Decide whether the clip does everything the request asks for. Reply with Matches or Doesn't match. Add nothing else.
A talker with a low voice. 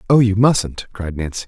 Matches